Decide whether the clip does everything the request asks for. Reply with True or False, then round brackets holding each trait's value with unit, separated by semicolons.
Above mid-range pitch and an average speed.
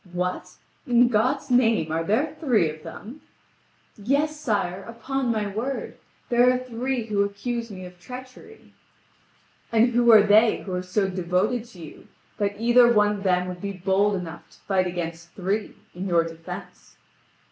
True (210 Hz; 165 wpm)